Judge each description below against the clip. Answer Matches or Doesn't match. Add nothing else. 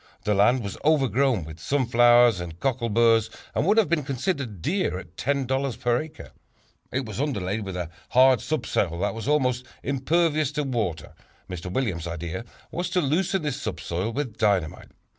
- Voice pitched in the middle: Doesn't match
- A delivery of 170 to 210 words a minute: Doesn't match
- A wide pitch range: Matches